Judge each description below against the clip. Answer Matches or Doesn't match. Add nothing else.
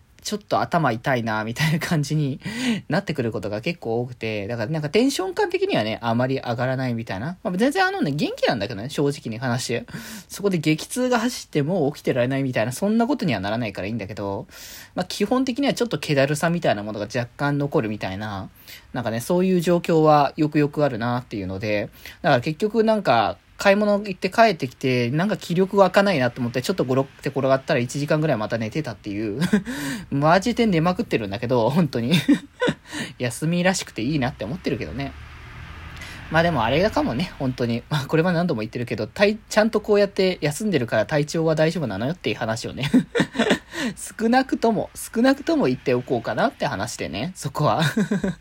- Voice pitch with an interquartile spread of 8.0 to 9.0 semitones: Matches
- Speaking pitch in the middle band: Matches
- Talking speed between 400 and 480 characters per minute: Matches